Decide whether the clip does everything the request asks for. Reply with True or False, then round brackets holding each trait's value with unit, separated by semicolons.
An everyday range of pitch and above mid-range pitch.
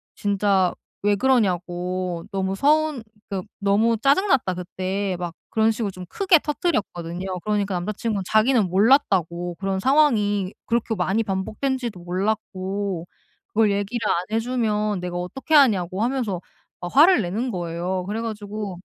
True (3.8 semitones; 200 Hz)